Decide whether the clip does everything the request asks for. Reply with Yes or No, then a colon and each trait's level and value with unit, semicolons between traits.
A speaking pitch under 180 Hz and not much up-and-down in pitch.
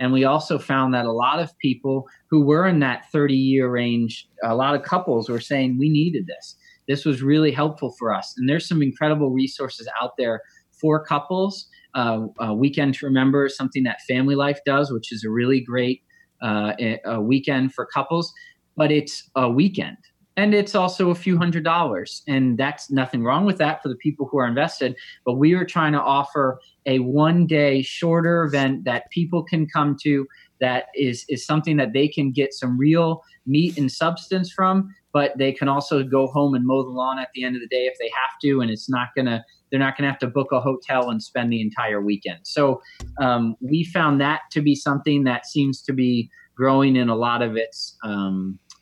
No: medium, 140 Hz; average, 3.2 semitones